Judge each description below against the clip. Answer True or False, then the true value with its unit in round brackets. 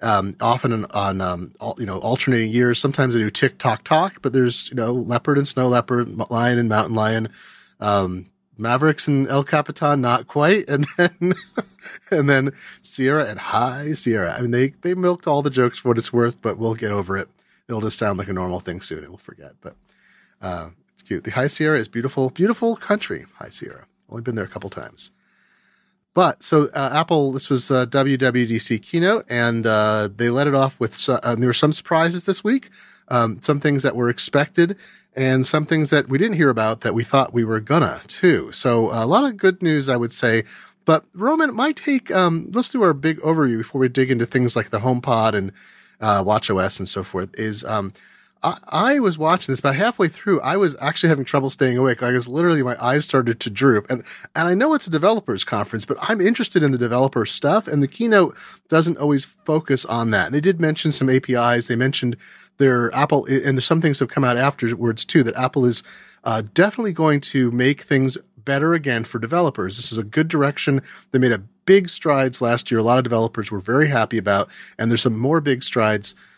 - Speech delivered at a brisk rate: True (220 wpm)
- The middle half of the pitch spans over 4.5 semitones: True (4.9 semitones)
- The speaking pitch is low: True (130 Hz)